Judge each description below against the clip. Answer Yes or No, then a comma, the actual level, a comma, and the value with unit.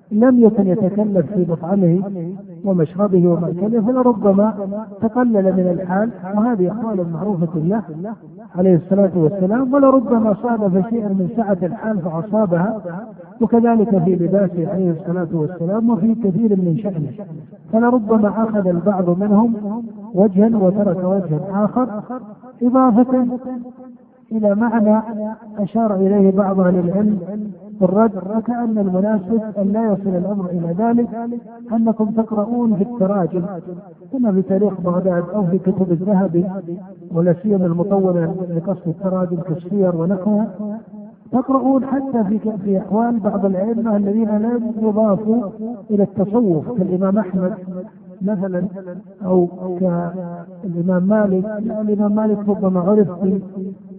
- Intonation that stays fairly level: No, average, 3.0 semitones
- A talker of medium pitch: No, high, 200 Hz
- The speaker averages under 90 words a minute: No, average, 115 wpm